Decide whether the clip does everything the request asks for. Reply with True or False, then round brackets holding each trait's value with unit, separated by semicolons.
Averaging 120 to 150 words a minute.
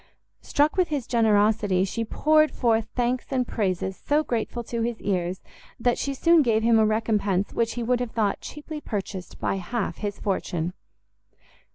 False (170 wpm)